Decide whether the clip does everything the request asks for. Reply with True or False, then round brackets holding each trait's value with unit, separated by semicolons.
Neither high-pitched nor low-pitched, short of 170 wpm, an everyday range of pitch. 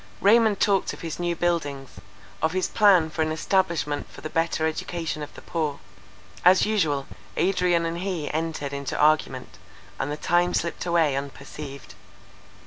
True (165 Hz; 155 wpm; 3.2 semitones)